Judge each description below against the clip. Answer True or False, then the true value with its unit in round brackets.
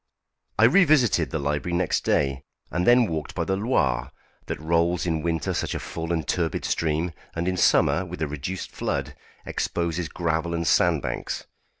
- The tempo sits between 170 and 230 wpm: True (175 wpm)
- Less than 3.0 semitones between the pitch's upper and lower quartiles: True (2.4 semitones)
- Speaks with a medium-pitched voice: False (85 Hz)